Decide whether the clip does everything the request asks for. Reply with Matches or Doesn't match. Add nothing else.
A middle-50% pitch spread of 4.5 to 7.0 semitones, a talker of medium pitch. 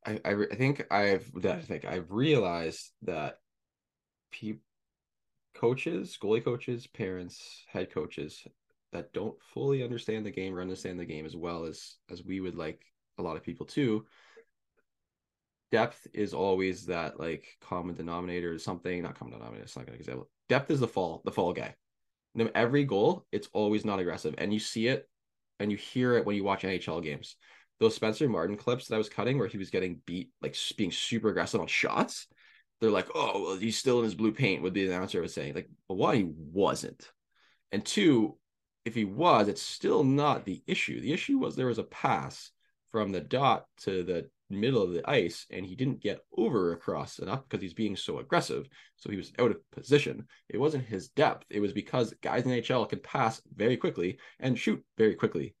Doesn't match